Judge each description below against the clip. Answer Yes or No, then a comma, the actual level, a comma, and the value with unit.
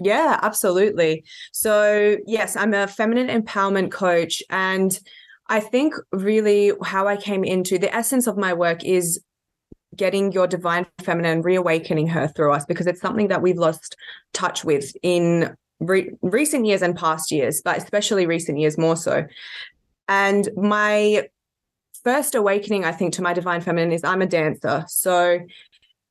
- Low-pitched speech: No, high, 190 Hz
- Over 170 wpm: No, average, 155 wpm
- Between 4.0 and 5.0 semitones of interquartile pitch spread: No, average, 3.1 semitones